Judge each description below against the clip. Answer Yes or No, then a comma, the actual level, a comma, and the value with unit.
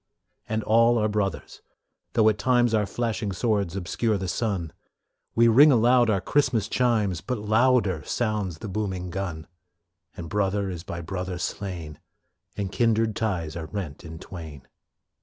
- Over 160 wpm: No, average, 150 wpm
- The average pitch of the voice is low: Yes, low, 105 Hz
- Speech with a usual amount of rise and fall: Yes, average, 3.9 semitones